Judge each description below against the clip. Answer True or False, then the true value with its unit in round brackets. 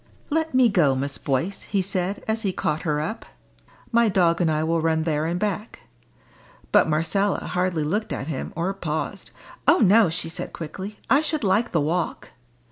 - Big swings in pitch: False (4.6 semitones)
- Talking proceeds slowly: False (185 wpm)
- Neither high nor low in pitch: True (180 Hz)